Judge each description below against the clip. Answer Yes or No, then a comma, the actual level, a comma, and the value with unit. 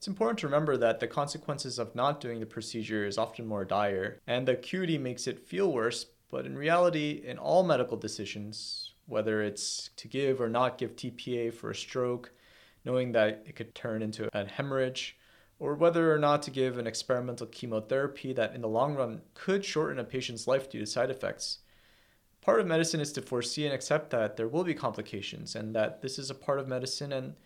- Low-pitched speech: Yes, low, 125 Hz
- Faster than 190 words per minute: Yes, fast, 205 wpm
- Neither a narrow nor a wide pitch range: Yes, average, 4.5 semitones